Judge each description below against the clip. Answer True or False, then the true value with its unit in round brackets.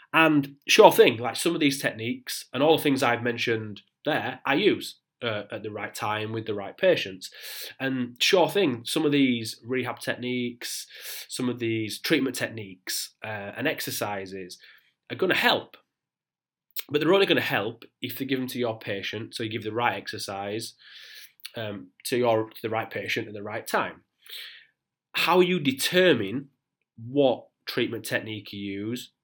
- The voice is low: True (120 Hz)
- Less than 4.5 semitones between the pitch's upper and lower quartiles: True (3.7 semitones)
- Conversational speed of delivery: True (170 wpm)